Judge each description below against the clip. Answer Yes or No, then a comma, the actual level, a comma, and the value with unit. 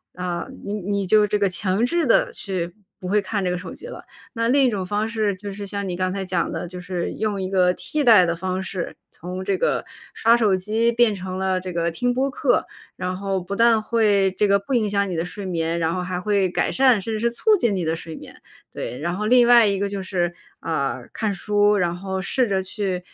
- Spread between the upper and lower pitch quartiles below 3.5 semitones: Yes, average, 2.9 semitones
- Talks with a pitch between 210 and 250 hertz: No, high, 195 Hz